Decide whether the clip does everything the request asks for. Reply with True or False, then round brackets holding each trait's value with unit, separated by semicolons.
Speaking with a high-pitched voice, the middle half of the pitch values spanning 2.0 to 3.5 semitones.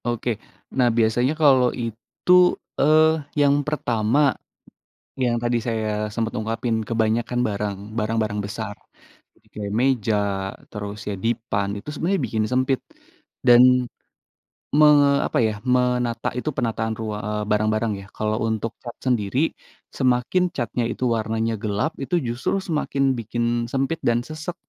False (115 Hz; 2.7 semitones)